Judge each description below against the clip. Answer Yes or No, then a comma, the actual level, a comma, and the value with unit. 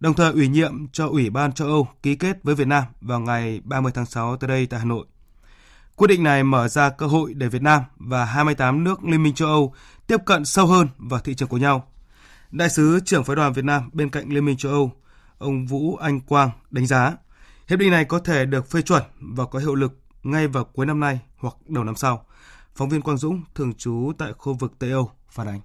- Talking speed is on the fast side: No, average, 240 wpm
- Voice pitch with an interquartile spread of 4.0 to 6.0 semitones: No, average, 3.2 semitones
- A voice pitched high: No, medium, 140 Hz